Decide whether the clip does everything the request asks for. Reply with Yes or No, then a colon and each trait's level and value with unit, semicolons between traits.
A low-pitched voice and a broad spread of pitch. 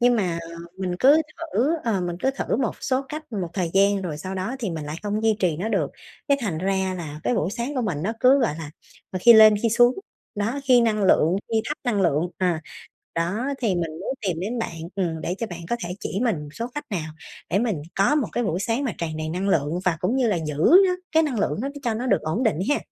No: high, 205 Hz; wide, 5.7 semitones